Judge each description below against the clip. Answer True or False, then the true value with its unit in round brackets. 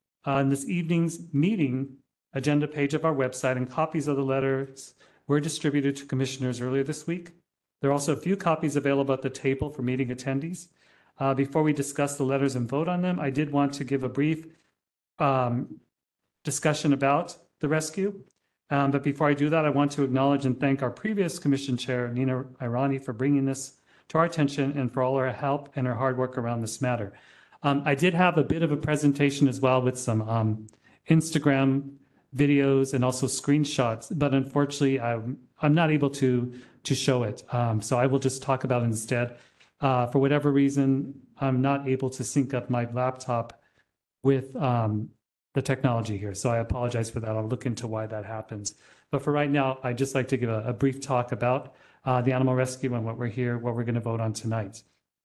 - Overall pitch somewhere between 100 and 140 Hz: True (135 Hz)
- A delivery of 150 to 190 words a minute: False (205 wpm)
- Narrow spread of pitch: True (2.3 semitones)